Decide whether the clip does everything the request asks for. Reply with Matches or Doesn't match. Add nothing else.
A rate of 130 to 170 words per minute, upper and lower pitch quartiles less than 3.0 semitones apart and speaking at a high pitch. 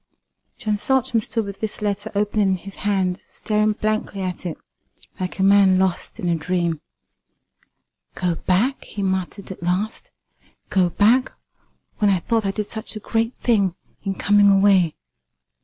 Matches